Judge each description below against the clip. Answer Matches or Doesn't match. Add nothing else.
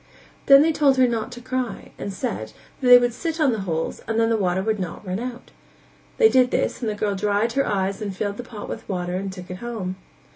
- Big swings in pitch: Doesn't match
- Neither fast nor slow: Doesn't match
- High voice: Matches